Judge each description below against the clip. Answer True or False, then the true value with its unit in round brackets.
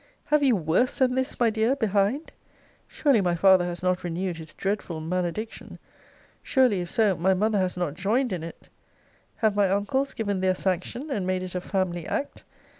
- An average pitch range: True (4.1 semitones)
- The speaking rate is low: False (185 wpm)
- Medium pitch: False (195 Hz)